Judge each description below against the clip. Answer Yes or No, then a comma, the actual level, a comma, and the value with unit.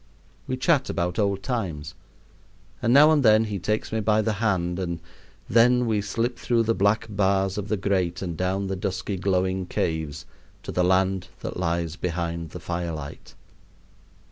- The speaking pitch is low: Yes, very low, 95 Hz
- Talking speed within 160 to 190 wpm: Yes, average, 170 wpm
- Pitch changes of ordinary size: Yes, average, 3.7 semitones